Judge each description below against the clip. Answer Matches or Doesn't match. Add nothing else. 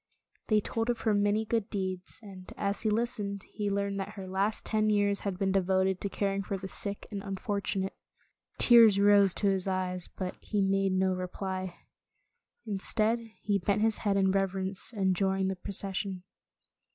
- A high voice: Matches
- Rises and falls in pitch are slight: Matches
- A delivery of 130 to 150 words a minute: Doesn't match